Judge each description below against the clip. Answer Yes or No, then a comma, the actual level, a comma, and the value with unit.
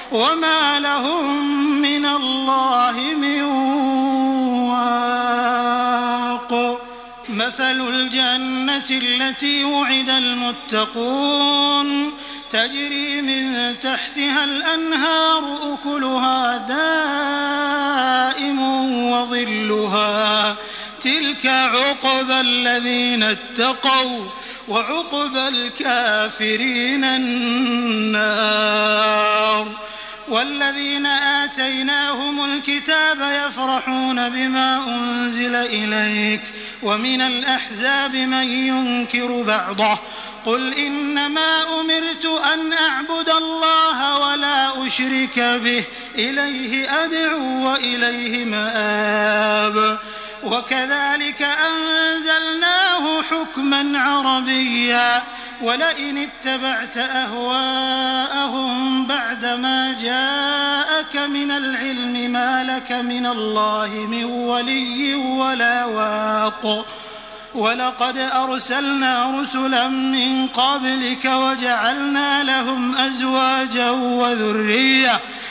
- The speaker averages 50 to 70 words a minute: Yes, slow, 65 wpm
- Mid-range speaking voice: No, very high, 260 Hz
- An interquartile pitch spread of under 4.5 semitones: Yes, average, 2.7 semitones